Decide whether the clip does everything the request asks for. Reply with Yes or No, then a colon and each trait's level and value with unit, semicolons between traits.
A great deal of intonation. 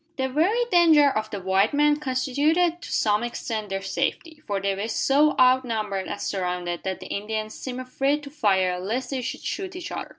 Yes: wide, 6.6 semitones